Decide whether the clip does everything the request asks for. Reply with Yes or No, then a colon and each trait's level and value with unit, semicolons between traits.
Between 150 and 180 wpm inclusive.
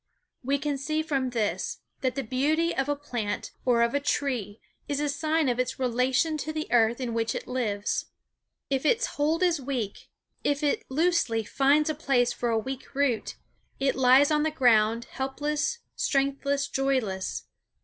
Yes: average, 170 wpm